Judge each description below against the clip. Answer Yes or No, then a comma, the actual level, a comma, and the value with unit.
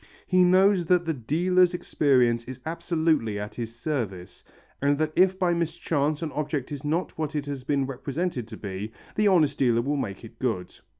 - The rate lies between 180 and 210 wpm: Yes, average, 185 wpm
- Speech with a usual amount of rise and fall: No, wide, 5.9 semitones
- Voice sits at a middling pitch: Yes, medium, 145 Hz